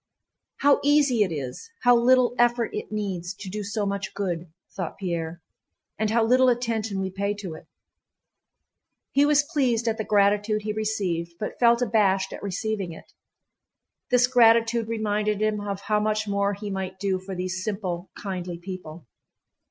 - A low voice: No, high, 205 Hz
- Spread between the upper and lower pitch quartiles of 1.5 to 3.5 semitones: Yes, average, 3.2 semitones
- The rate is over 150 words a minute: Yes, average, 165 wpm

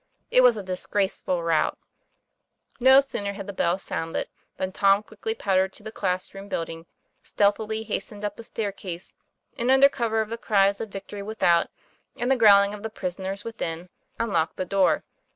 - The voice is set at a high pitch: Yes, high, 200 Hz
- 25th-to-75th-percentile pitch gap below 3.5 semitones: Yes, average, 2.9 semitones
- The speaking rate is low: No, average, 175 wpm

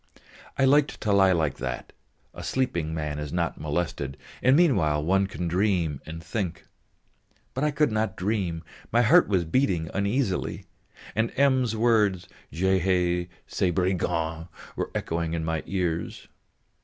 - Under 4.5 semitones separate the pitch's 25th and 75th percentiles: No, average, 5.2 semitones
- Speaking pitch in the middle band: No, very low, 90 Hz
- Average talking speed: Yes, average, 145 wpm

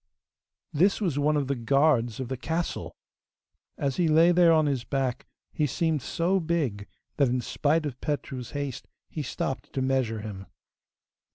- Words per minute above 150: Yes, average, 165 wpm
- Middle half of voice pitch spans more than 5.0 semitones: No, average, 4.0 semitones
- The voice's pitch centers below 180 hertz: Yes, medium, 140 Hz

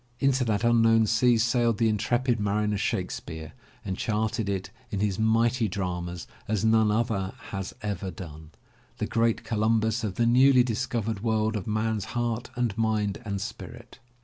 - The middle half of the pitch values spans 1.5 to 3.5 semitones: Yes, narrow, 2.5 semitones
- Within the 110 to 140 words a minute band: No, average, 155 wpm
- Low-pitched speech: Yes, low, 110 Hz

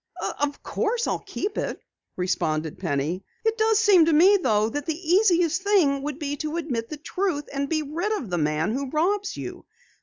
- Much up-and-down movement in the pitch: Yes, wide, 7.5 semitones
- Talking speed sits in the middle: Yes, average, 190 wpm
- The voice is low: No, very high, 305 Hz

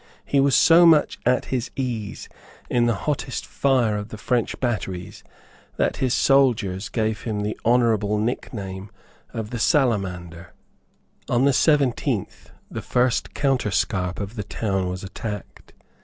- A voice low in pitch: Yes, low, 115 Hz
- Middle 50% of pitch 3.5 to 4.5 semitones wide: Yes, average, 4.2 semitones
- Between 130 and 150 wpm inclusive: Yes, average, 140 wpm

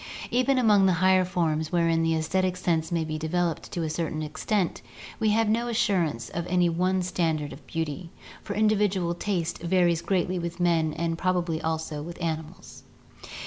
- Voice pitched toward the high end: No, medium, 175 Hz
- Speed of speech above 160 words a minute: Yes, average, 170 wpm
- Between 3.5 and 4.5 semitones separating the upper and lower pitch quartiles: No, narrow, 2.6 semitones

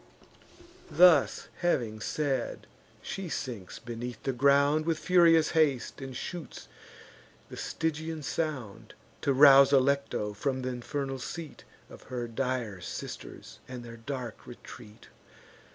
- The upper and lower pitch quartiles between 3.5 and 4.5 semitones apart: Yes, average, 4.2 semitones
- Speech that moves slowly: Yes, slow, 120 wpm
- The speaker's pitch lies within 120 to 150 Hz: Yes, low, 135 Hz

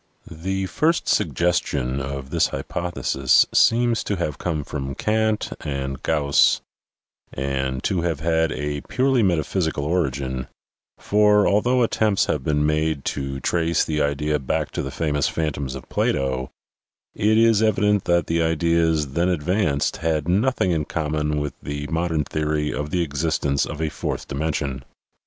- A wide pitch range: No, average, 3.9 semitones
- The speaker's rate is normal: Yes, average, 150 wpm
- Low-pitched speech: Yes, very low, 80 Hz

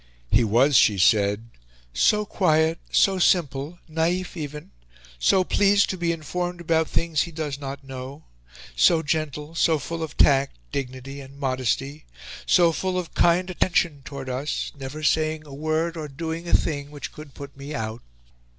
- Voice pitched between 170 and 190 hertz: No, medium, 150 Hz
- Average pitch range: Yes, average, 3.6 semitones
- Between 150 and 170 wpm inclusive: Yes, average, 160 wpm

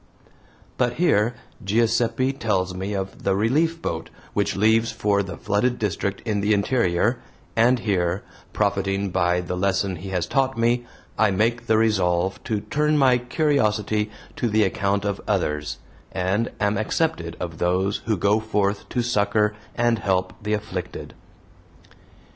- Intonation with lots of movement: No, average, 3.3 semitones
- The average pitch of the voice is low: Yes, low, 105 Hz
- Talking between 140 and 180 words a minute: Yes, average, 150 wpm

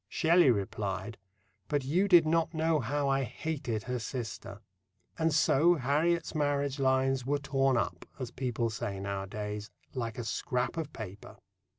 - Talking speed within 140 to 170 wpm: Yes, average, 150 wpm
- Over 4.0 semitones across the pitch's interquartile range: Yes, average, 5.0 semitones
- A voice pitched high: No, low, 135 Hz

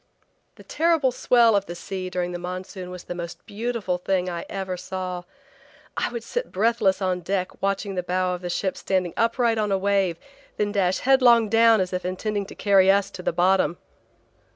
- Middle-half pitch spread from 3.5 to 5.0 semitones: No, average, 3.0 semitones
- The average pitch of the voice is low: No, high, 190 Hz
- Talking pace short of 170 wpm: No, average, 195 wpm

